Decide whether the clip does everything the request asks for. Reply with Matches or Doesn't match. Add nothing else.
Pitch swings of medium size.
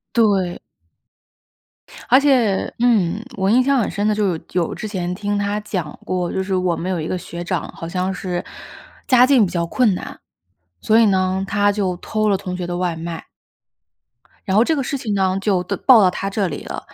Matches